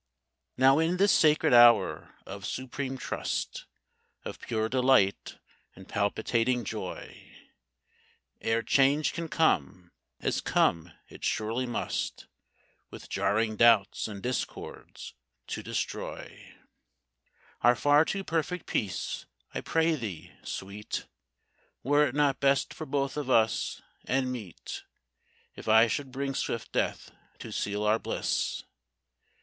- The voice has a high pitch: No, low, 125 Hz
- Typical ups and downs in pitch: Yes, average, 4.7 semitones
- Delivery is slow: Yes, slow, 120 wpm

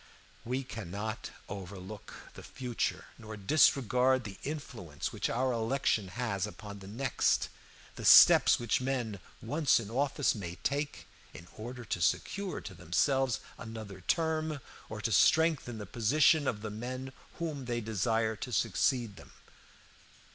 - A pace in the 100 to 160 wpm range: Yes, average, 140 wpm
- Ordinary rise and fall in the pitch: Yes, average, 4.4 semitones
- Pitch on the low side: Yes, low, 115 Hz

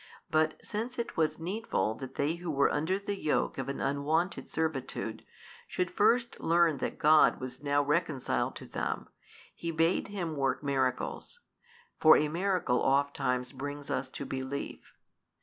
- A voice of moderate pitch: Yes, medium, 155 Hz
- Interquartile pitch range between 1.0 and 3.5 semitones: No, average, 4.0 semitones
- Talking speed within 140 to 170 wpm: Yes, average, 160 wpm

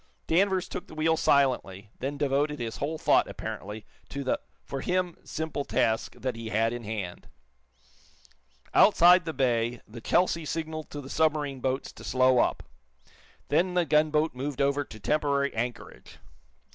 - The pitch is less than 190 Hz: Yes, medium, 140 Hz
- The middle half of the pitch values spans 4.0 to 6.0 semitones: Yes, average, 4.6 semitones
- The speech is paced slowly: No, average, 155 wpm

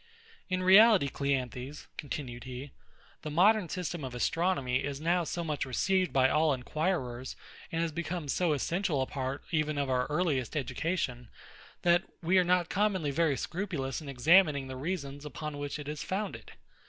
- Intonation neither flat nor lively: Yes, average, 4.6 semitones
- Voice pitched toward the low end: No, medium, 150 Hz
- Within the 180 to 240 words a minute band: No, average, 165 wpm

